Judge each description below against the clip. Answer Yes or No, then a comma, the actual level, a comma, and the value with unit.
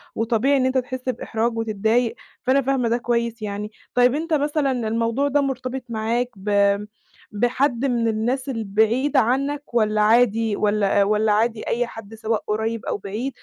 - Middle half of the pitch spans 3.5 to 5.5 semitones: No, average, 3.0 semitones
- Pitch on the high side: Yes, high, 235 Hz